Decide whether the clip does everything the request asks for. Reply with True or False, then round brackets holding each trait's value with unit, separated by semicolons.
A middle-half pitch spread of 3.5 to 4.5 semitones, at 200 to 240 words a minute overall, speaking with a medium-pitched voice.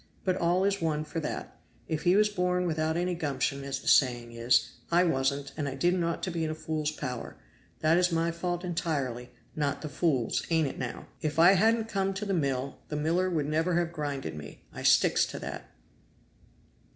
True (4.1 semitones; 205 wpm; 160 Hz)